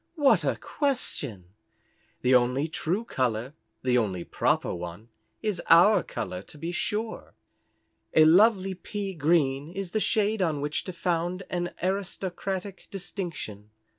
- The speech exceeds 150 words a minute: No, slow, 135 wpm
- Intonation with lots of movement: Yes, wide, 7.2 semitones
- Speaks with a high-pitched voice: No, medium, 175 Hz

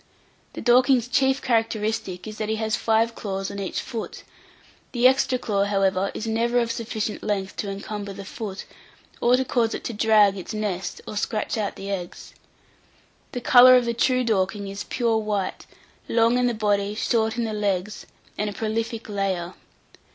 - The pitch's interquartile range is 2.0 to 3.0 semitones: Yes, average, 2.7 semitones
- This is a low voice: No, high, 215 Hz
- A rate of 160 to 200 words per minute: Yes, average, 180 wpm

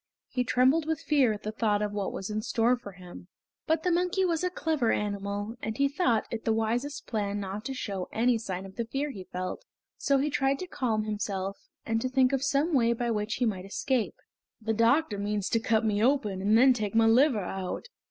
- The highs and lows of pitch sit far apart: No, average, 4.6 semitones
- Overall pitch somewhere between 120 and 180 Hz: No, high, 225 Hz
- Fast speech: Yes, fast, 225 wpm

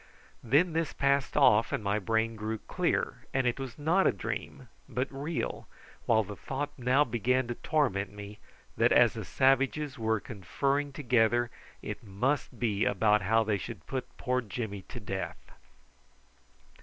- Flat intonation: No, average, 4.3 semitones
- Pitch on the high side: No, low, 120 Hz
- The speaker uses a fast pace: No, average, 155 wpm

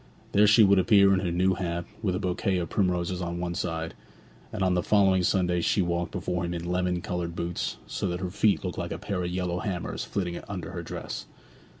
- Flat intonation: Yes, narrow, 1.7 semitones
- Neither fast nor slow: No, fast, 225 wpm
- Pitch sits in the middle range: No, very low, 90 Hz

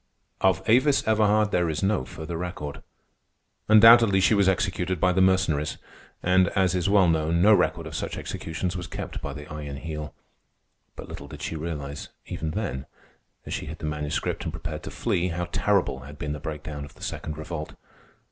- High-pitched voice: No, very low, 85 Hz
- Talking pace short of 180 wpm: No, average, 185 wpm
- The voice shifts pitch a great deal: No, average, 3.8 semitones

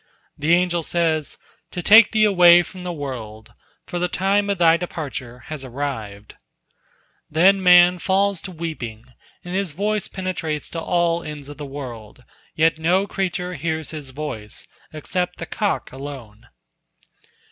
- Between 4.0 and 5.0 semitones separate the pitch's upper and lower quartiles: Yes, average, 4.3 semitones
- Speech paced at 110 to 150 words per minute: Yes, average, 145 wpm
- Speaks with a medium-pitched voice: Yes, medium, 165 Hz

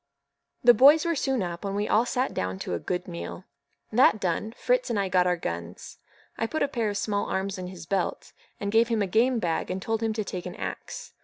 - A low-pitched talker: No, high, 200 Hz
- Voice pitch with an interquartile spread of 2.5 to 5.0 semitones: Yes, average, 4.5 semitones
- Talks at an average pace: No, fast, 235 wpm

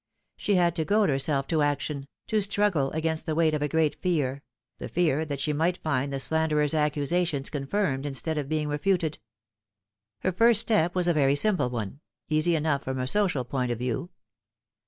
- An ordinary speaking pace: Yes, average, 185 wpm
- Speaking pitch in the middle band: Yes, medium, 155 Hz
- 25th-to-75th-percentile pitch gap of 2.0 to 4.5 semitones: Yes, average, 3.9 semitones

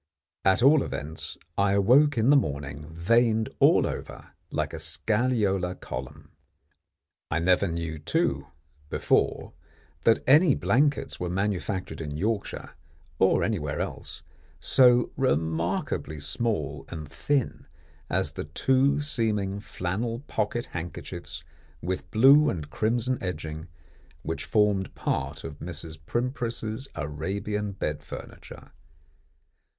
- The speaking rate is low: Yes, slow, 110 wpm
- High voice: No, very low, 95 Hz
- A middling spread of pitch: No, wide, 6.6 semitones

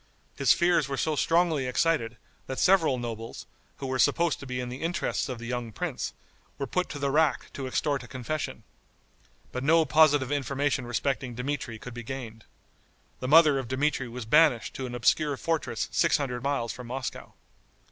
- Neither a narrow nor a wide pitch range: Yes, average, 3.5 semitones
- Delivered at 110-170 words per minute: No, average, 180 wpm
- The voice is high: No, low, 135 Hz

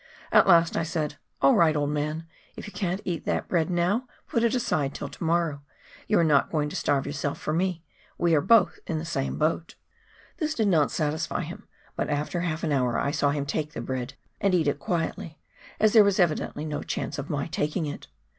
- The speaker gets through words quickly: Yes, fast, 220 wpm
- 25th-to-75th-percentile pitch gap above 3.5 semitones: No, average, 3.2 semitones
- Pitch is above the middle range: No, medium, 160 Hz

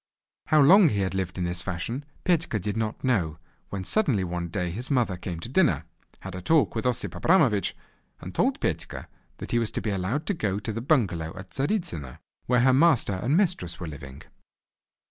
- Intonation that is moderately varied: No, wide, 7.1 semitones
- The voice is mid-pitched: No, low, 105 Hz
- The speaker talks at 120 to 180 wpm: No, average, 200 wpm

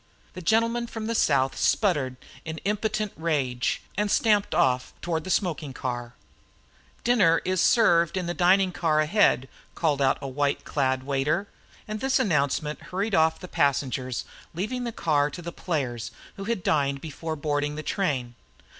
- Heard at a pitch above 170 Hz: No, medium, 160 Hz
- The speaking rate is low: No, average, 155 wpm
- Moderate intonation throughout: No, wide, 6.0 semitones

